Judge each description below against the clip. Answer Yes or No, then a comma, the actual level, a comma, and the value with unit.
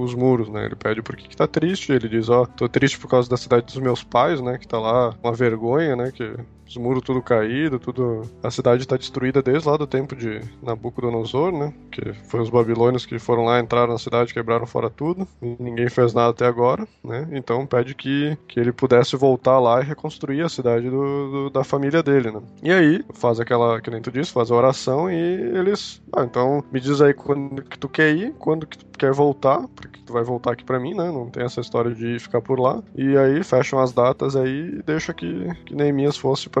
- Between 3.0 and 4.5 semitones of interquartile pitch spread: No, narrow, 2.6 semitones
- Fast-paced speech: Yes, fast, 230 wpm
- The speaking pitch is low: Yes, low, 125 Hz